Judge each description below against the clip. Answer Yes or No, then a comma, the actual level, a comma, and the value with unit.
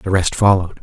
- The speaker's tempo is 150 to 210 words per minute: No, fast, 220 wpm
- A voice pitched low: Yes, very low, 95 Hz